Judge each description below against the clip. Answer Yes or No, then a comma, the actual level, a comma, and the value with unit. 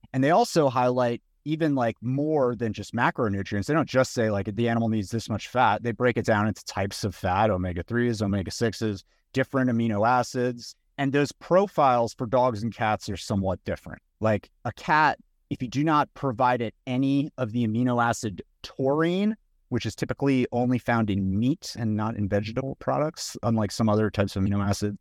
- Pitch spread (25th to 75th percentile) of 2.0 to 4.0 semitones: Yes, average, 3.6 semitones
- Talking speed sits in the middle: Yes, average, 190 wpm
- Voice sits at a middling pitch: No, low, 115 Hz